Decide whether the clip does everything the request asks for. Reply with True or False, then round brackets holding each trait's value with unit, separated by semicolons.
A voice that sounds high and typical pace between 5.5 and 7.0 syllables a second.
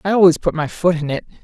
False (170 Hz; 6.8 syllables/s)